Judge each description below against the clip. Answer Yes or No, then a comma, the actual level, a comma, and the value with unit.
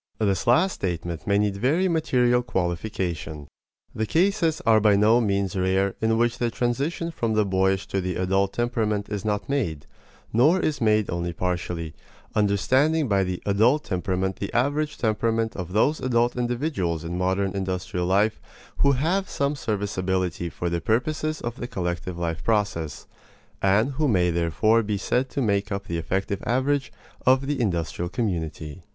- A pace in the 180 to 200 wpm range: No, average, 160 wpm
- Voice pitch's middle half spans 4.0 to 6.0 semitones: Yes, average, 5.0 semitones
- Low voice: Yes, low, 105 Hz